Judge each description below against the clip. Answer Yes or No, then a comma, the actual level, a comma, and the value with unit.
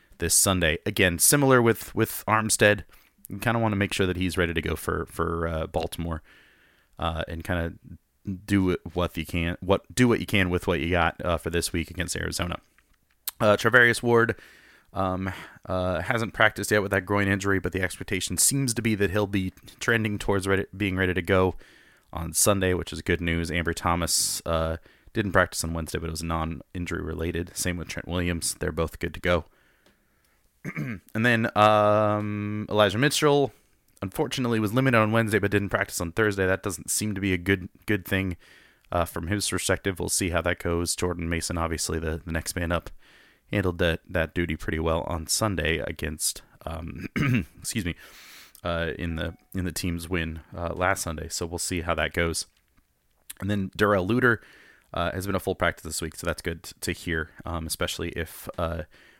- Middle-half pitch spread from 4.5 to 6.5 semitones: No, average, 3.4 semitones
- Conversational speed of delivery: Yes, average, 195 wpm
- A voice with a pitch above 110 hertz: No, very low, 90 Hz